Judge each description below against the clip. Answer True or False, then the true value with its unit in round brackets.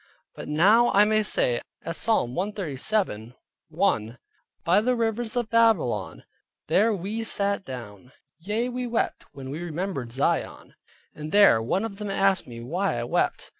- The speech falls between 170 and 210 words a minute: False (145 wpm)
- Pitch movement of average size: False (8.3 semitones)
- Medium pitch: False (195 Hz)